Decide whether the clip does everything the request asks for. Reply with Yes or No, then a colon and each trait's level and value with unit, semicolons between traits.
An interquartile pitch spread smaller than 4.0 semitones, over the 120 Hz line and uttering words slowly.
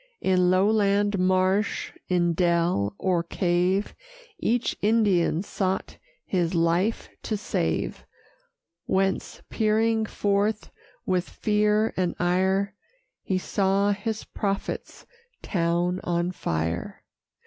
Yes: average, 2.8 semitones; high, 190 Hz; slow, 95 wpm